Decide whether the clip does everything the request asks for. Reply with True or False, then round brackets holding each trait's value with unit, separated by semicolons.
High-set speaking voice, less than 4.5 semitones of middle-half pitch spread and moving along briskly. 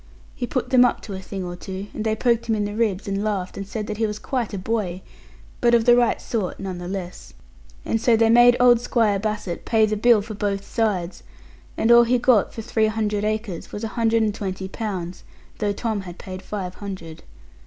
True (210 Hz; 2.9 semitones; 230 wpm)